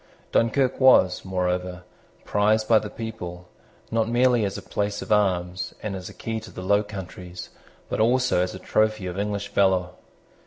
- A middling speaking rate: Yes, average, 170 wpm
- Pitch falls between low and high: No, low, 100 Hz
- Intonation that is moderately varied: Yes, average, 3.3 semitones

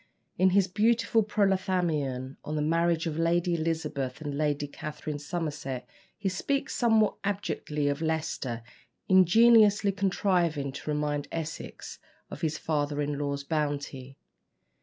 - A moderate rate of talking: No, slow, 125 wpm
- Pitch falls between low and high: Yes, medium, 160 Hz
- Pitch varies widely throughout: No, average, 4.5 semitones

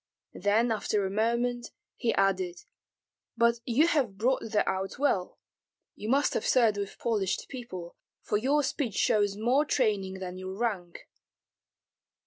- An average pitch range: Yes, average, 3.9 semitones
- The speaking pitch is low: No, high, 215 Hz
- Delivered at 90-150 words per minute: Yes, average, 140 wpm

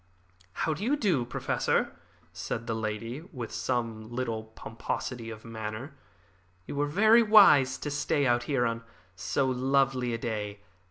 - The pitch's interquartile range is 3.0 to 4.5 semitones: Yes, average, 4.2 semitones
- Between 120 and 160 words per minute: Yes, average, 150 wpm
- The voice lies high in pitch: No, low, 125 Hz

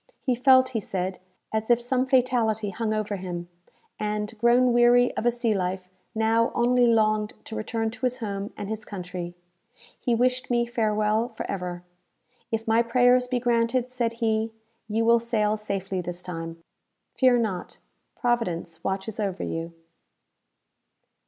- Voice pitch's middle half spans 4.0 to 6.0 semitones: No, average, 3.3 semitones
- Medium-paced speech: Yes, average, 150 wpm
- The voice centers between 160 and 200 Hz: No, high, 220 Hz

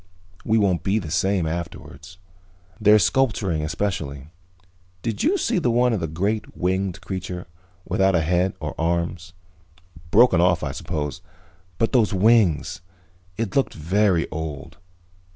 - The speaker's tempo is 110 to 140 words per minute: Yes, slow, 135 wpm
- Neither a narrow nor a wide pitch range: Yes, average, 4.4 semitones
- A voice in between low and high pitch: No, very low, 90 Hz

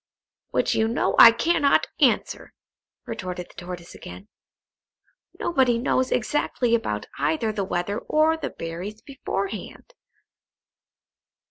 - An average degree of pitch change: No, wide, 6.0 semitones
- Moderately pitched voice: No, high, 215 Hz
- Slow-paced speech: Yes, slow, 110 wpm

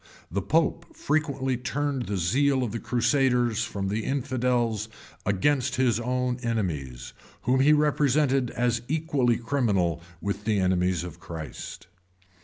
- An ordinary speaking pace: No, slow, 130 wpm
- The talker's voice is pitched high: No, low, 120 Hz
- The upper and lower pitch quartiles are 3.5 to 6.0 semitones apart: Yes, average, 5.1 semitones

